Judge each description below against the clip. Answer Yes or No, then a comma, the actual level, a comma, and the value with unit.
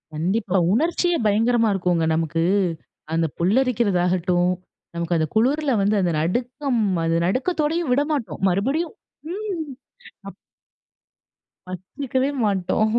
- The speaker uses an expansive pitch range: Yes, wide, 7.6 semitones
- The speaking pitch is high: Yes, high, 220 Hz